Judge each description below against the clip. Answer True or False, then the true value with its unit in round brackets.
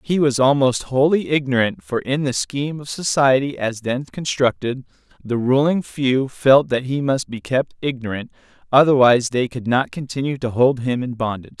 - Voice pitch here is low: True (130 Hz)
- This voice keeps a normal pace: True (175 wpm)